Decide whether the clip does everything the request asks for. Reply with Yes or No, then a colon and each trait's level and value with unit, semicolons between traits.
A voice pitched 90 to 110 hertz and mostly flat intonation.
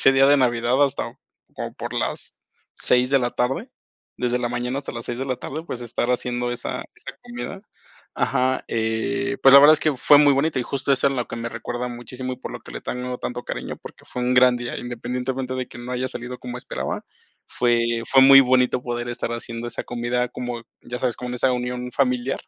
No: low, 125 Hz; narrow, 1.4 semitones